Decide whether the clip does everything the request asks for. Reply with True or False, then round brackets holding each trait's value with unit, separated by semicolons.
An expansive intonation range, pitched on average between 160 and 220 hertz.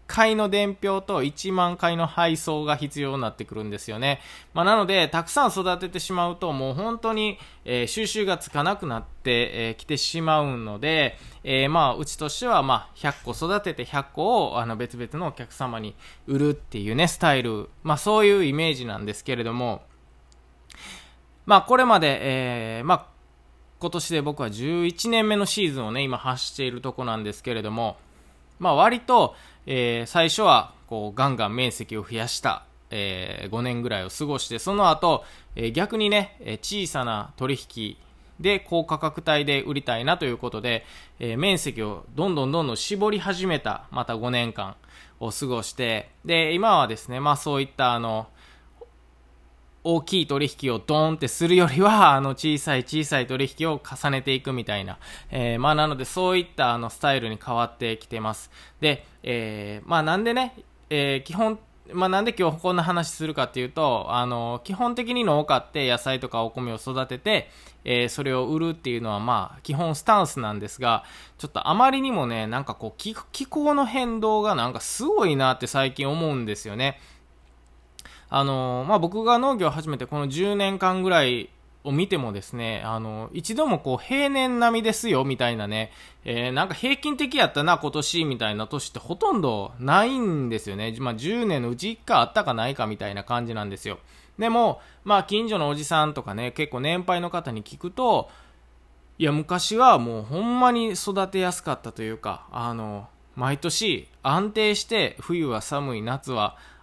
False (7.5 semitones; 140 Hz)